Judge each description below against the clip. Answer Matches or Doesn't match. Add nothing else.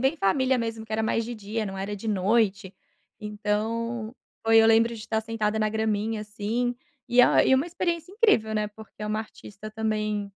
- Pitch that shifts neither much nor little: Doesn't match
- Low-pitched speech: Doesn't match